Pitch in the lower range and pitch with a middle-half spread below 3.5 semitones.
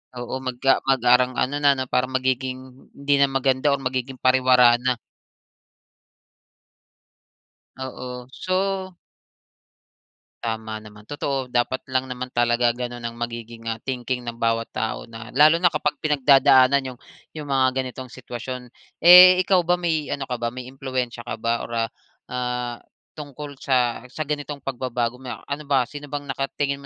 Yes: low, 130 Hz; narrow, 2.6 semitones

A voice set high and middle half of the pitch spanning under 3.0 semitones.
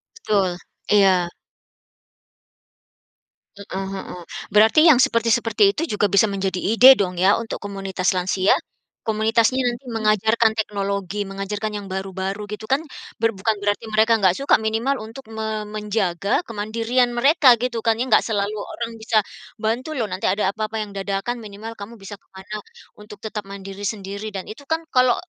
Yes: high, 215 Hz; narrow, 2.5 semitones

